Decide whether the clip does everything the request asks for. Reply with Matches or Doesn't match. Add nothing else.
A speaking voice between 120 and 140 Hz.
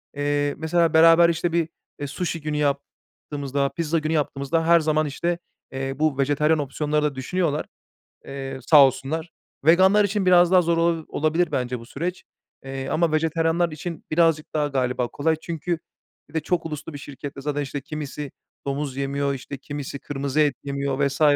Doesn't match